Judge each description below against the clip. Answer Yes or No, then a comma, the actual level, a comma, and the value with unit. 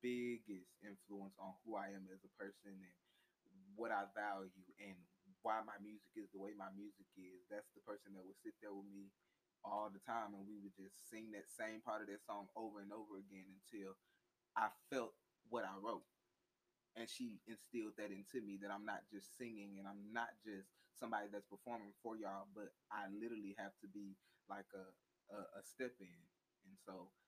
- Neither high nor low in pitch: No, low, 100 Hz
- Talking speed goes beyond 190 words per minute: Yes, average, 200 wpm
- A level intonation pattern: Yes, narrow, 1.8 semitones